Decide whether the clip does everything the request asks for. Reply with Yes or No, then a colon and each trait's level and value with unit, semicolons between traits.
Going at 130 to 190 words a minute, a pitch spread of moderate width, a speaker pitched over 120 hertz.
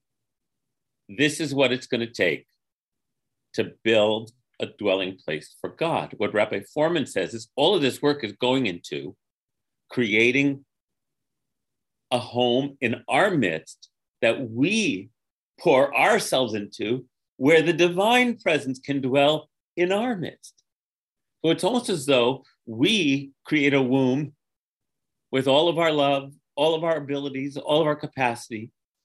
Yes: average, 140 wpm; average, 3.6 semitones; low, 135 Hz